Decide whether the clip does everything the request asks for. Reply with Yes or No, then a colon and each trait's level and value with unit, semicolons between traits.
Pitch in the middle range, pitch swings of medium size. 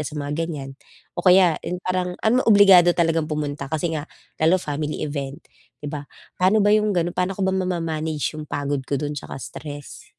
Yes: medium, 160 Hz; average, 3.8 semitones